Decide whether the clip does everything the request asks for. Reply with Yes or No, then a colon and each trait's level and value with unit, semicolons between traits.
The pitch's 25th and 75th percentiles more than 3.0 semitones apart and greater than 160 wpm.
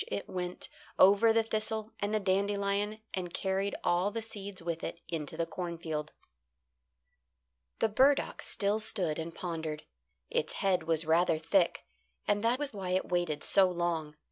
No: average, 3.7 semitones; average, 155 wpm